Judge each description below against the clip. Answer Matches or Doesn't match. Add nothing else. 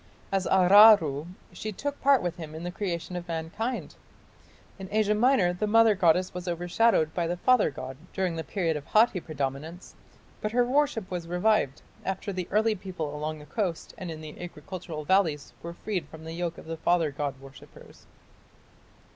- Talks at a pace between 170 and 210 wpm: Matches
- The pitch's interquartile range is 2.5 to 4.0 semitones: Doesn't match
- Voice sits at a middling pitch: Matches